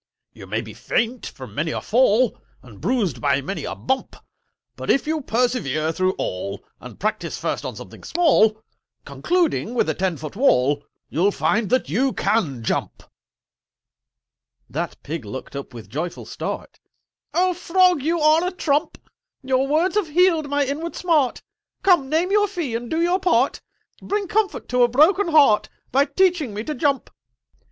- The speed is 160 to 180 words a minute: Yes, average, 165 wpm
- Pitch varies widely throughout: Yes, wide, 8.9 semitones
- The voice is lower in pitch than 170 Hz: No, very high, 270 Hz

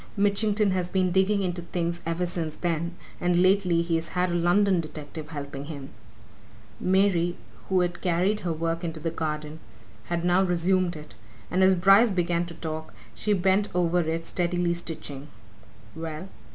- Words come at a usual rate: Yes, average, 160 wpm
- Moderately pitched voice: Yes, medium, 175 Hz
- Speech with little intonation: Yes, narrow, 2.1 semitones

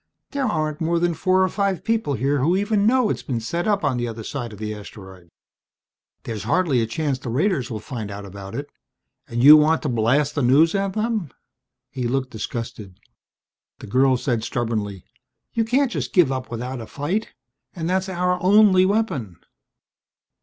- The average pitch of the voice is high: No, medium, 145 Hz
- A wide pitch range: Yes, wide, 8.0 semitones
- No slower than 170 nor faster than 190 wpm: Yes, average, 185 wpm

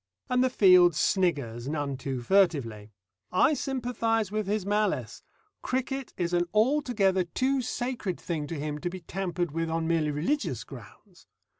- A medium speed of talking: Yes, average, 150 wpm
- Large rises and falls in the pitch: Yes, wide, 6.6 semitones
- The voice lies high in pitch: No, medium, 180 Hz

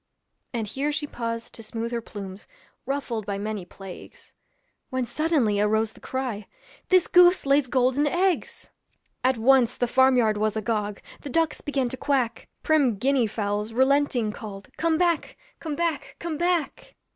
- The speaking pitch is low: No, very high, 250 Hz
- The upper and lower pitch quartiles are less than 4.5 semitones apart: No, average, 5.1 semitones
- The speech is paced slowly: No, average, 155 wpm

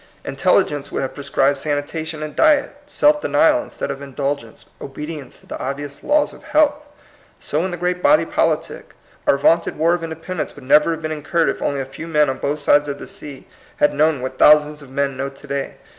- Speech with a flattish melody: No, average, 3.1 semitones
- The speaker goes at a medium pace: No, fast, 215 wpm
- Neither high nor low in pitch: Yes, medium, 150 Hz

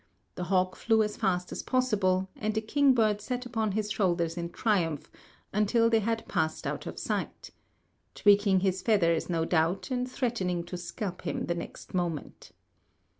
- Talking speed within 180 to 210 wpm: No, average, 165 wpm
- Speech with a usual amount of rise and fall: Yes, average, 4.0 semitones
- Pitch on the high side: Yes, high, 195 Hz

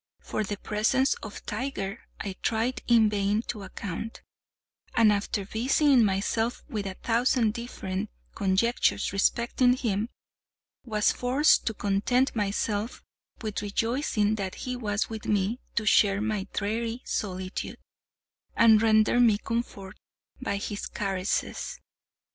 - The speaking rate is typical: No, slow, 125 wpm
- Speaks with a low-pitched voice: No, high, 215 Hz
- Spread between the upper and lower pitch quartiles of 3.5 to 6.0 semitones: No, average, 2.7 semitones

